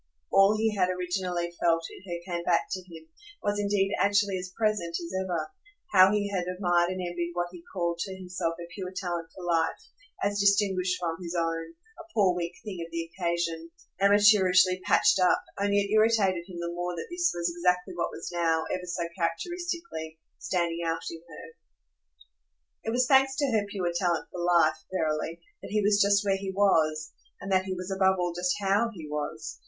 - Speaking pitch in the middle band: Yes, medium, 180 Hz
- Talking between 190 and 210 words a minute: Yes, average, 195 wpm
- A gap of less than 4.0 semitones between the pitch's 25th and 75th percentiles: Yes, average, 2.8 semitones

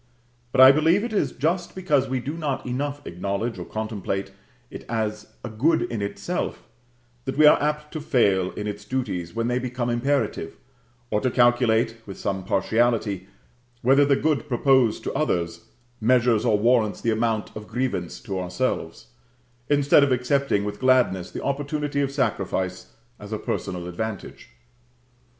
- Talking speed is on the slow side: No, average, 160 wpm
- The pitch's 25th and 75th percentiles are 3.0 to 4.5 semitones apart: No, average, 5.1 semitones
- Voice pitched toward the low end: Yes, low, 120 Hz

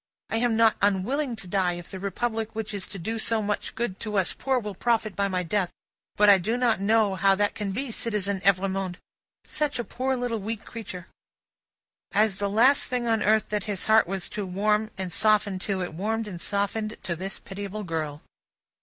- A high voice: Yes, high, 210 Hz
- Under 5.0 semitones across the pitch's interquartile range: Yes, average, 2.7 semitones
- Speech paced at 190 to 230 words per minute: Yes, fast, 205 wpm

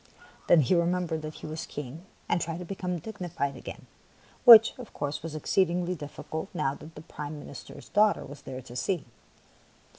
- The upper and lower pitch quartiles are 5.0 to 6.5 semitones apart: No, average, 3.5 semitones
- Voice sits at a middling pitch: Yes, medium, 160 Hz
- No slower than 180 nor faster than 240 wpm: Yes, average, 190 wpm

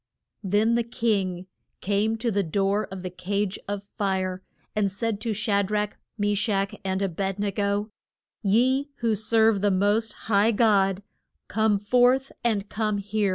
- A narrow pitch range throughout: Yes, narrow, 2.0 semitones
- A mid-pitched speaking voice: No, high, 205 Hz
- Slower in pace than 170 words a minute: Yes, average, 160 wpm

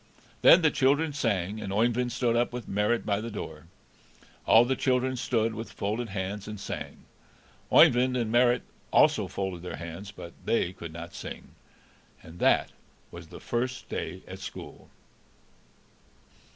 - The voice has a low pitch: Yes, low, 115 Hz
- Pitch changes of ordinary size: Yes, average, 4.2 semitones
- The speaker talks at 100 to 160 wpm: Yes, average, 150 wpm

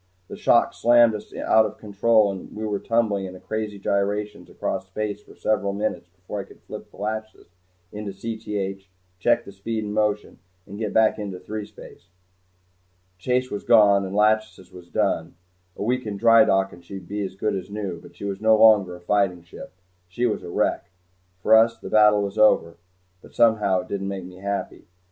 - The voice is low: Yes, low, 105 Hz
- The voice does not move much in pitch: Yes, narrow, 2.0 semitones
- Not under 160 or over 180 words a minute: No, average, 190 wpm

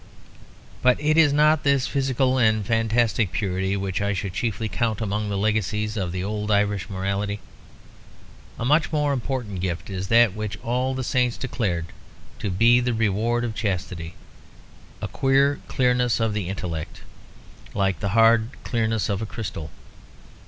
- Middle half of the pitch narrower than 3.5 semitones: No, average, 3.8 semitones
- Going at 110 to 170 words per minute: Yes, average, 155 wpm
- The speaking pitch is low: Yes, low, 110 Hz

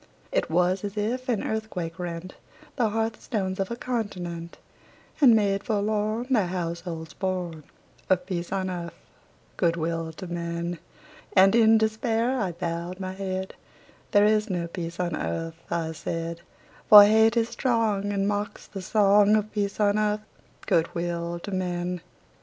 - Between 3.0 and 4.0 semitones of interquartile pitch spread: Yes, average, 3.7 semitones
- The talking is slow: No, average, 155 wpm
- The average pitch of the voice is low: No, high, 190 Hz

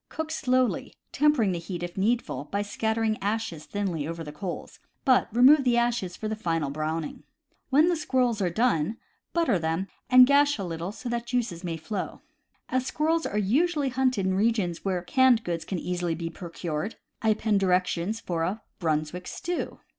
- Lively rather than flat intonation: Yes, wide, 6.4 semitones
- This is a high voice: Yes, high, 205 Hz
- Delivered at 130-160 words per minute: No, average, 180 wpm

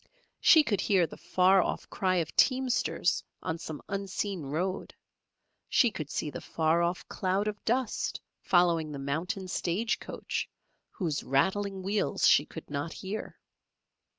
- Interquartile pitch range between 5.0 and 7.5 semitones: No, average, 3.9 semitones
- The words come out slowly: No, average, 145 wpm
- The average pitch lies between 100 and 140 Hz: No, medium, 185 Hz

